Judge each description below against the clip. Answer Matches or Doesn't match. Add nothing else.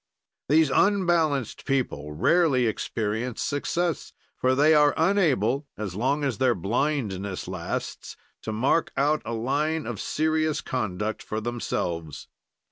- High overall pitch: Doesn't match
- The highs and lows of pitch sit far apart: Matches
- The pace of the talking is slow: Matches